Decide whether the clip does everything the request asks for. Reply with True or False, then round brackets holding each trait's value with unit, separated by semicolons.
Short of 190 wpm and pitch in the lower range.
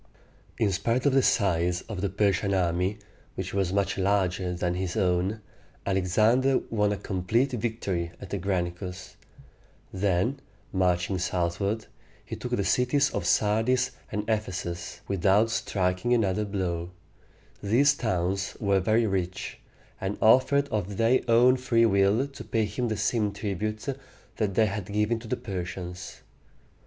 True (145 wpm; 100 Hz)